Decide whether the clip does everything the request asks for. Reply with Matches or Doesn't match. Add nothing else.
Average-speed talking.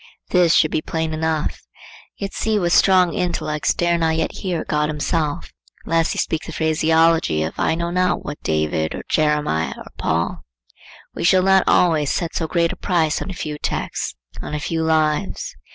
Matches